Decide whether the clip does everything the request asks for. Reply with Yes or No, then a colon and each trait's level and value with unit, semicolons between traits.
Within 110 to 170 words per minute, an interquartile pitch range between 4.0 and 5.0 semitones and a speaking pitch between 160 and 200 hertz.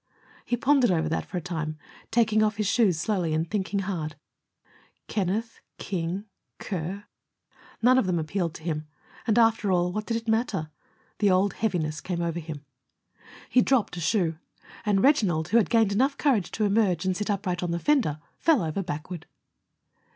No: average, 180 wpm; average, 4.7 semitones; high, 190 Hz